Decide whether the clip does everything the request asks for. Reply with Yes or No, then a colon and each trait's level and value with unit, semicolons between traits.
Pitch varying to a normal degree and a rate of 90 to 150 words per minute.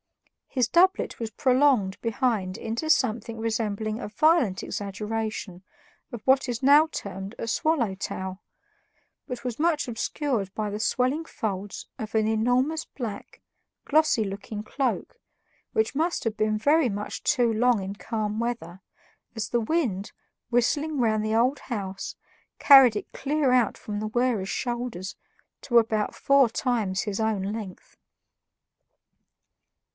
Yes: average, 3.7 semitones; slow, 135 wpm